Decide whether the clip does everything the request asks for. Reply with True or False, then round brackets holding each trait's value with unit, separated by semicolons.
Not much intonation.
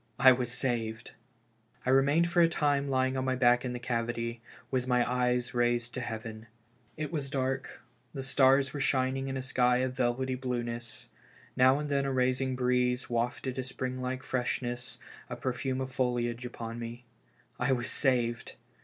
True (1.5 semitones)